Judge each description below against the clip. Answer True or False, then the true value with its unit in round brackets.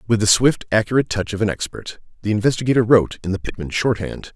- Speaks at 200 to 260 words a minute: True (205 wpm)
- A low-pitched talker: True (105 Hz)